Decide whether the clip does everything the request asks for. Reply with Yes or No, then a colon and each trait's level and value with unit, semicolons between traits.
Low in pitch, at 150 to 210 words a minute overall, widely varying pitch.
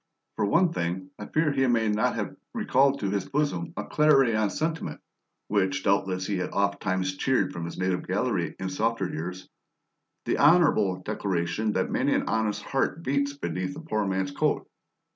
Yes: low, 105 Hz; average, 170 wpm; wide, 6.5 semitones